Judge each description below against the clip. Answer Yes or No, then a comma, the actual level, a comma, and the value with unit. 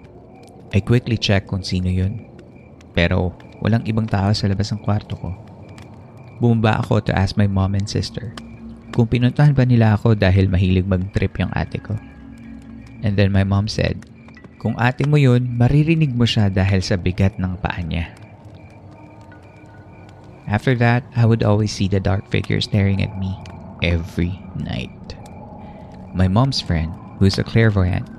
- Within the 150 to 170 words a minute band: Yes, fast, 155 wpm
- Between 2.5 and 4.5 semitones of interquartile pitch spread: Yes, average, 3.3 semitones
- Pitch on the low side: Yes, low, 105 Hz